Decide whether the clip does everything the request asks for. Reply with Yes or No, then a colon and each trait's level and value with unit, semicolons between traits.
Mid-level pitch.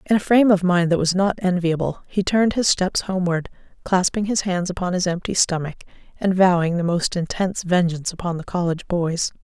Yes: medium, 180 Hz